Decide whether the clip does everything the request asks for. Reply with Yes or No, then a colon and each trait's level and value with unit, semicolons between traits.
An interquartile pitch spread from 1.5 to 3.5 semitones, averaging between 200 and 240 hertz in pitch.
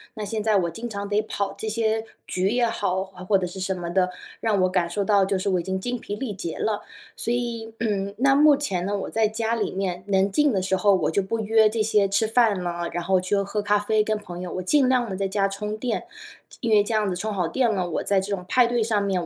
Yes: average, 2.8 semitones; high, 205 Hz